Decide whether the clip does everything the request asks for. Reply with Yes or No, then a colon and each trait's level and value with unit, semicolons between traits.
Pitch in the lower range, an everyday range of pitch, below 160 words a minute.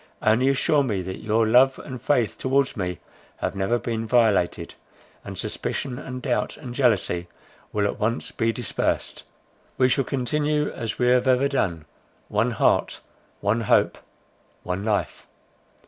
Yes: low, 120 Hz; average, 3.7 semitones; average, 145 wpm